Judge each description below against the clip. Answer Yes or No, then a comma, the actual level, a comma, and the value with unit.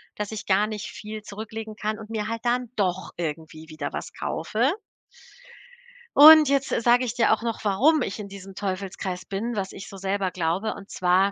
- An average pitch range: Yes, average, 3.1 semitones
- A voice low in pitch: No, high, 210 Hz